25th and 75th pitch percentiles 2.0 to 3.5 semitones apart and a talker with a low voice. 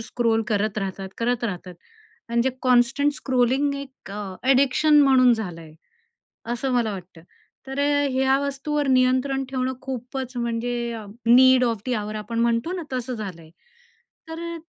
No: average, 3.0 semitones; high, 245 Hz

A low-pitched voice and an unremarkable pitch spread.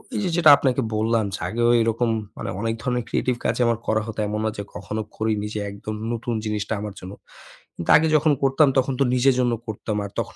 Yes: low, 115 Hz; average, 3.1 semitones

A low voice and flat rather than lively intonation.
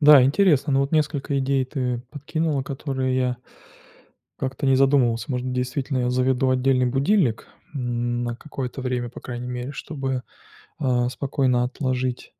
Yes: low, 130 Hz; narrow, 1.8 semitones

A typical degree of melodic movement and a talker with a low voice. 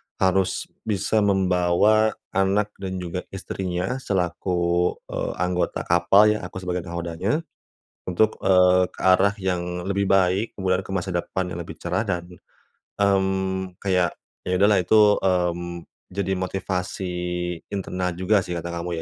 No: narrow, 1.7 semitones; very low, 95 Hz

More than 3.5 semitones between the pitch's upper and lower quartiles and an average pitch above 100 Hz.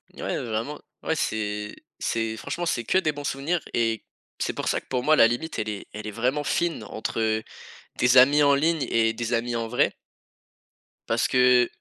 Yes: average, 4.5 semitones; low, 120 Hz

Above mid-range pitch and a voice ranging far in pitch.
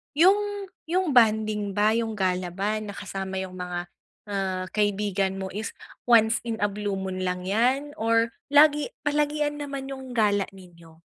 Yes: high, 215 Hz; wide, 5.9 semitones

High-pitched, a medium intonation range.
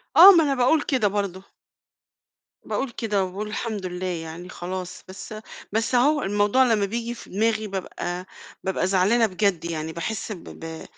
Yes: high, 200 Hz; average, 3.9 semitones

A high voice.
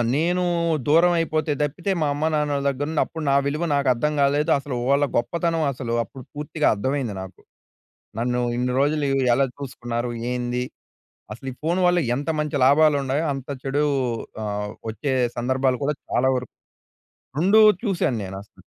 No: medium, 140 Hz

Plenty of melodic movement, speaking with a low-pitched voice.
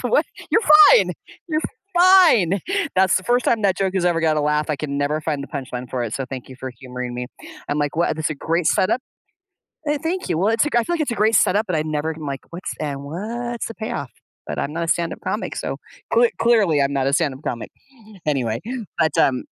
No: wide, 7.6 semitones; medium, 160 Hz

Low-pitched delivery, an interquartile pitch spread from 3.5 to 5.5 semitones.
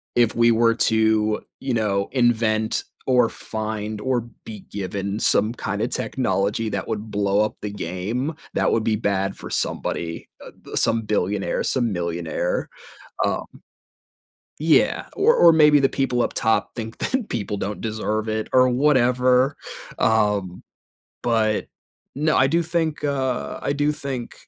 Yes: low, 110 Hz; average, 3.8 semitones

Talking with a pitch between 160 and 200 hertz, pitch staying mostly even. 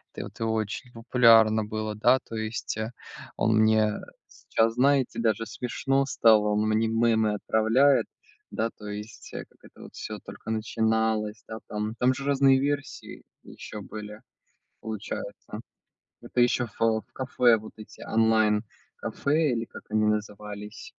No: low, 110 Hz; narrow, 2.1 semitones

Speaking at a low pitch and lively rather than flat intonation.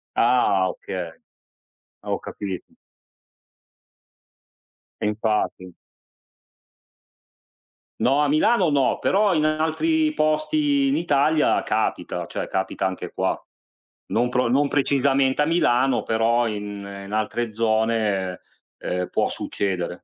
Yes: low, 120 Hz; wide, 6.9 semitones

